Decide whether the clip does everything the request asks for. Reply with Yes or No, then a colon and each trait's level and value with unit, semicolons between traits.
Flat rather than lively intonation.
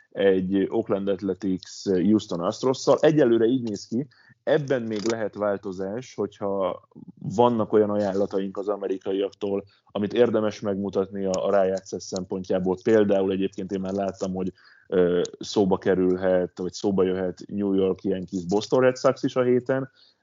Yes: narrow, 2.3 semitones